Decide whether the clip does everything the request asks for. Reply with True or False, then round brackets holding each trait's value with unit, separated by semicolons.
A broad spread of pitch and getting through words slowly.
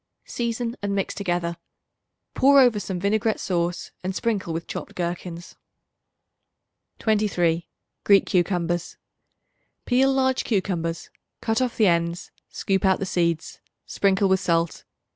False (4.1 semitones; 125 wpm)